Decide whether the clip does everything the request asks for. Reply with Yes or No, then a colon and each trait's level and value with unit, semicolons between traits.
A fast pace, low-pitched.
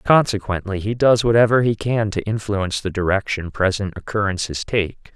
No: average, 150 wpm; low, 105 Hz